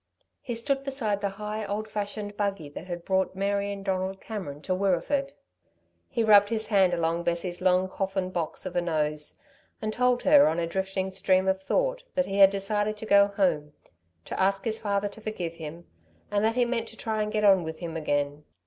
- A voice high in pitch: Yes, high, 195 Hz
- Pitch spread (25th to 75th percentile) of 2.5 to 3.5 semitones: Yes, average, 3.2 semitones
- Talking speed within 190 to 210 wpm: Yes, fast, 205 wpm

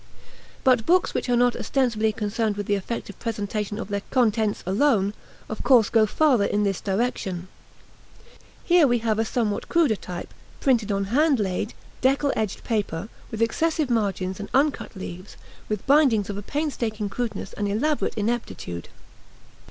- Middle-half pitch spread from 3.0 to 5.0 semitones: Yes, average, 3.7 semitones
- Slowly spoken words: No, average, 155 wpm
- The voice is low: No, high, 220 Hz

